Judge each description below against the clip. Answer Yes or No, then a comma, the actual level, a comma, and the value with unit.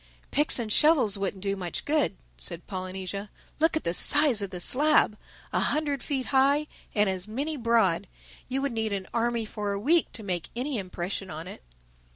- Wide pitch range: Yes, wide, 6.6 semitones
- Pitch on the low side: No, high, 220 Hz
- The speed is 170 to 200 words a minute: Yes, average, 190 wpm